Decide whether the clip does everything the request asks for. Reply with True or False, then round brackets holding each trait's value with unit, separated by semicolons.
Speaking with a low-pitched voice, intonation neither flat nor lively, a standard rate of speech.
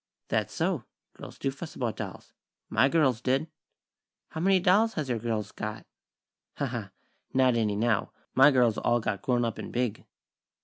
True (125 Hz; 4.0 semitones; 170 wpm)